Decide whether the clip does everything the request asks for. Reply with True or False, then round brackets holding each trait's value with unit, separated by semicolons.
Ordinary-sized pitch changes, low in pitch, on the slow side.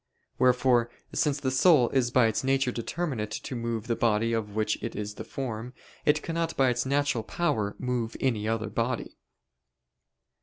False (3.1 semitones; 120 Hz; 165 wpm)